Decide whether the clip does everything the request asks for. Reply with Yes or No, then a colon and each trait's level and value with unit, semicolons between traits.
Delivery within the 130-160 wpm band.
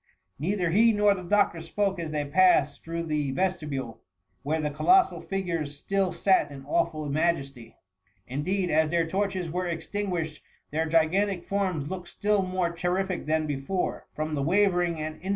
No: average, 170 wpm